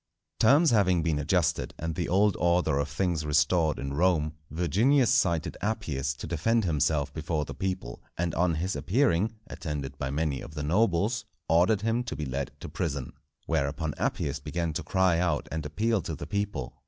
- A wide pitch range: No, average, 4.5 semitones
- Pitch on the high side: No, very low, 85 Hz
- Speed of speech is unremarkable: Yes, average, 180 wpm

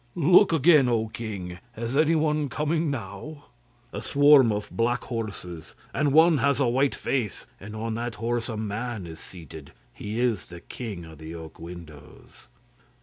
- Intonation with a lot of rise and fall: Yes, wide, 6.8 semitones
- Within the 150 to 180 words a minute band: Yes, average, 160 wpm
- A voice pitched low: Yes, low, 115 Hz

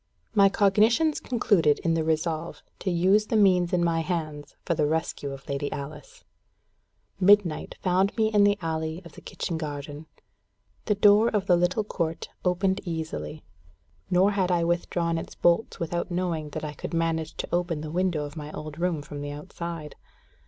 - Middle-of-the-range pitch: Yes, medium, 170 Hz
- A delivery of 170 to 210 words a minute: Yes, average, 175 wpm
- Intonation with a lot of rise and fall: No, average, 3.4 semitones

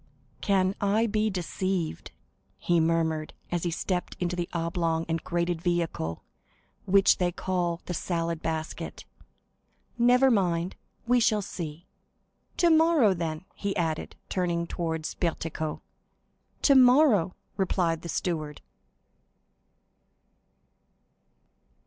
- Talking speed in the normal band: No, slow, 100 wpm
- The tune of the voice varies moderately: Yes, average, 3.1 semitones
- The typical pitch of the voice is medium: Yes, medium, 175 Hz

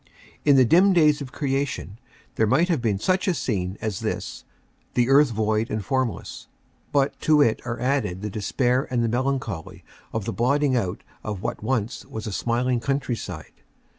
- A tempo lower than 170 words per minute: No, average, 175 wpm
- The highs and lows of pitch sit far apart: No, average, 4.3 semitones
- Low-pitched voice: Yes, low, 125 Hz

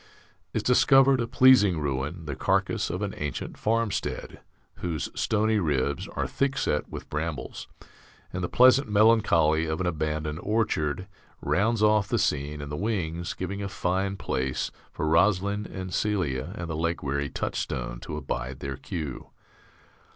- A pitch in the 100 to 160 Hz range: No, very low, 90 Hz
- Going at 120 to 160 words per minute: Yes, average, 150 wpm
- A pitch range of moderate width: No, wide, 5.9 semitones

